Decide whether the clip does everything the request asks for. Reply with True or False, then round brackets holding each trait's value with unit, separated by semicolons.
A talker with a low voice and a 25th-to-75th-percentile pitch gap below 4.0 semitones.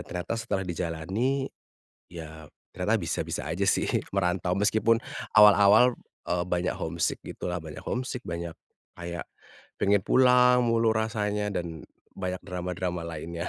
False (90 Hz; 4.3 semitones)